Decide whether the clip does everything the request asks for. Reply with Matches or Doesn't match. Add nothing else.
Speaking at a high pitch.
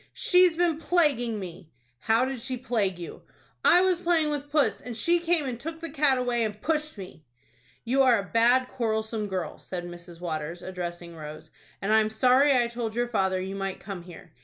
Matches